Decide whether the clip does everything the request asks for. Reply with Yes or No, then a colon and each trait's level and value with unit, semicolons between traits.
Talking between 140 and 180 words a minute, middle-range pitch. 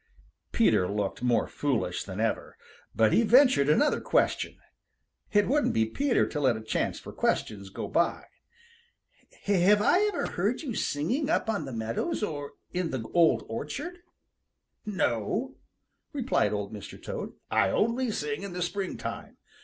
Yes: average, 150 wpm; medium, 170 Hz